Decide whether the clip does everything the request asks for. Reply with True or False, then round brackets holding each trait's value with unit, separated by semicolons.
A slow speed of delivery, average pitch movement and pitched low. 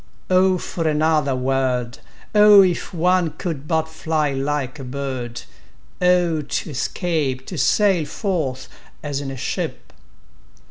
False (120 wpm; 4.7 semitones; 155 Hz)